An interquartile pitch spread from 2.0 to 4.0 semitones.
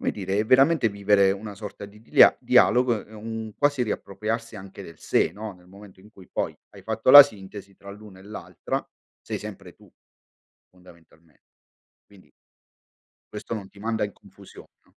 Yes: narrow, 2.5 semitones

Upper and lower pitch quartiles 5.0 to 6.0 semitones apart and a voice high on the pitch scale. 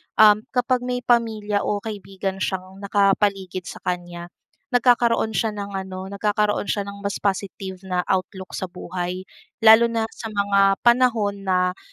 No: average, 2.7 semitones; high, 200 Hz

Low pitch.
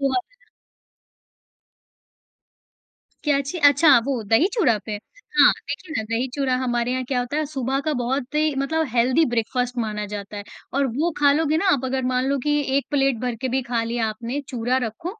No: very high, 260 Hz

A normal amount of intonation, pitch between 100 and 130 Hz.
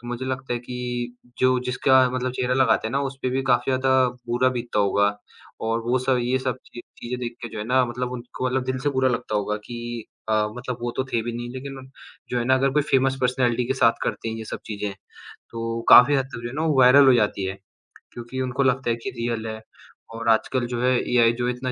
No: narrow, 1.8 semitones; low, 125 Hz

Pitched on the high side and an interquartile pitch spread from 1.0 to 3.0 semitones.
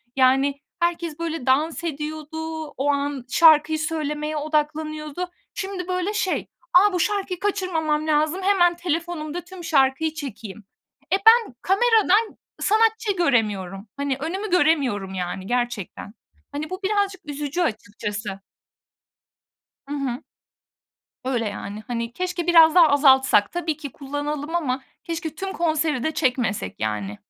No: very high, 310 Hz; average, 4.7 semitones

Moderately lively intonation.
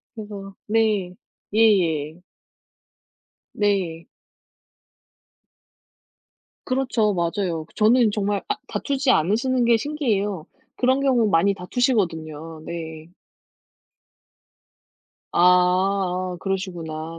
Yes: average, 4.8 semitones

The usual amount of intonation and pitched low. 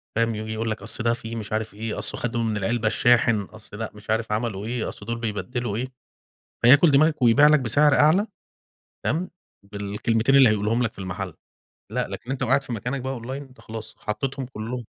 Yes: average, 3.1 semitones; low, 115 Hz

